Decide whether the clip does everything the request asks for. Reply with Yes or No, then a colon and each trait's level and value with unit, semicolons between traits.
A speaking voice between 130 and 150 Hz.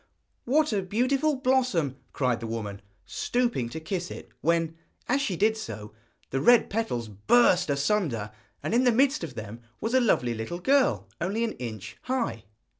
No: medium, 180 Hz